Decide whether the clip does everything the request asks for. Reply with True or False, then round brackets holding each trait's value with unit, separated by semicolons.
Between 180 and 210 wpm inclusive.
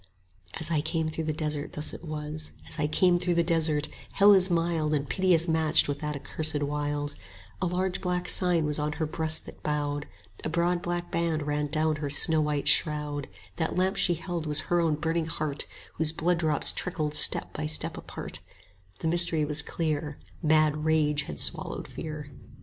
True (195 wpm)